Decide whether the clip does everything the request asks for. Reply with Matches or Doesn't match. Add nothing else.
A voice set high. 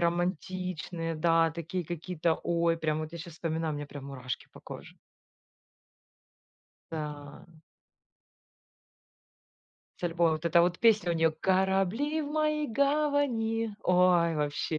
Doesn't match